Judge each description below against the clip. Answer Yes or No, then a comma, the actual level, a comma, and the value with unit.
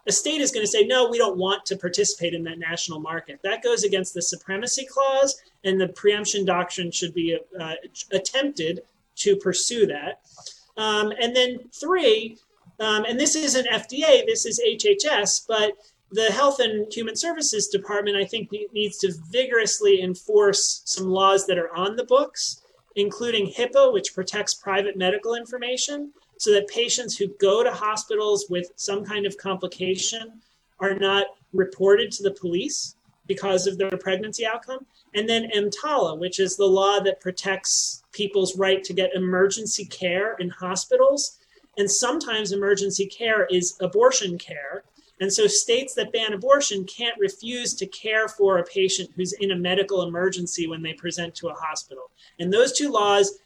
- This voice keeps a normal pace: Yes, average, 165 wpm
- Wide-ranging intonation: No, average, 4.0 semitones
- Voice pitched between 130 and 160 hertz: No, high, 200 Hz